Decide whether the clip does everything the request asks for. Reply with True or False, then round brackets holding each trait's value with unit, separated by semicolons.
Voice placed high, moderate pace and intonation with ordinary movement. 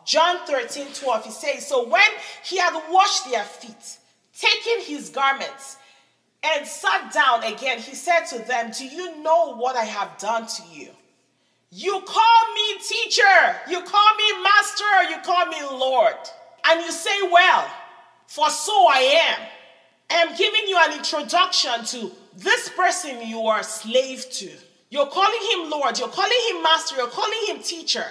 False (325 Hz; 165 wpm; 7.1 semitones)